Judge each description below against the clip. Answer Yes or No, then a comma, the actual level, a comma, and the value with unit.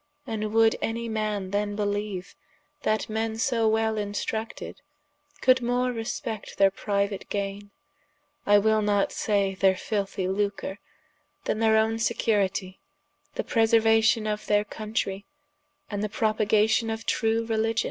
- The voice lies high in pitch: Yes, high, 215 Hz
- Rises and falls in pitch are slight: Yes, narrow, 1.6 semitones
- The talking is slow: Yes, slow, 130 wpm